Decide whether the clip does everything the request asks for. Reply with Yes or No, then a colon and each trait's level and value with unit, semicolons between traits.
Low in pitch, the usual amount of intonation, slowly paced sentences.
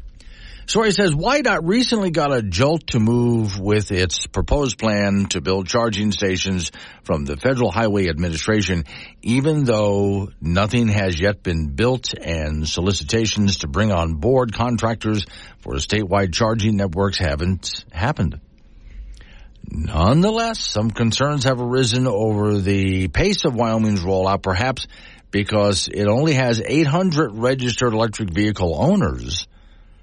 Yes: low, 105 Hz; average, 4.6 semitones; slow, 130 wpm